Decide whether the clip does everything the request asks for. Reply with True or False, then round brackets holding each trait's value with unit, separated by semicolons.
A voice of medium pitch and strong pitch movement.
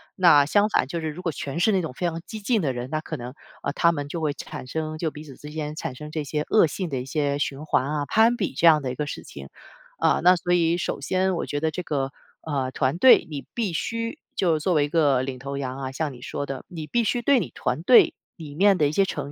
False (155 Hz; 3.9 semitones)